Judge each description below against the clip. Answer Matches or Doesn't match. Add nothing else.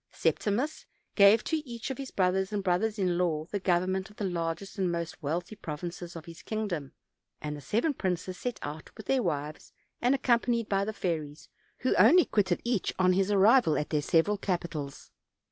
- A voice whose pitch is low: Doesn't match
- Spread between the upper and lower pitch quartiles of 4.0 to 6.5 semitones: Matches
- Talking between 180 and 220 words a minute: Matches